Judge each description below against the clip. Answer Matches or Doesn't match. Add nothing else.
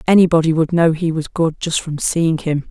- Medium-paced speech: Doesn't match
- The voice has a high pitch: Doesn't match